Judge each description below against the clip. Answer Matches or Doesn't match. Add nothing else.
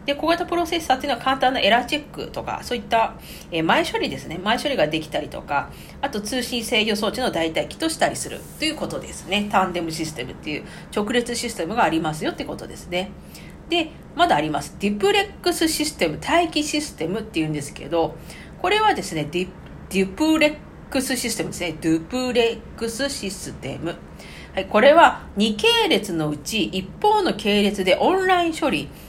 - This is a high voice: Matches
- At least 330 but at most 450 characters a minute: Matches